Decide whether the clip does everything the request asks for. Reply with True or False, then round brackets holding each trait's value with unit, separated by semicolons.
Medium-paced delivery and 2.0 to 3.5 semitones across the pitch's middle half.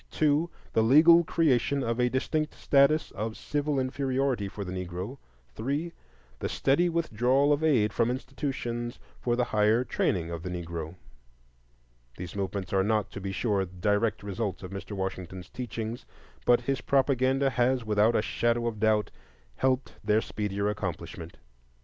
False (150 wpm; 5.1 semitones)